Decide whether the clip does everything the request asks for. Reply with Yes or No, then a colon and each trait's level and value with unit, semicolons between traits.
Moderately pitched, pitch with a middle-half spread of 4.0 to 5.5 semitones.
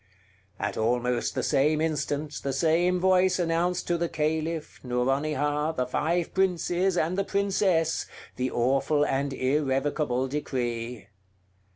Yes: medium, 150 Hz; average, 4.3 semitones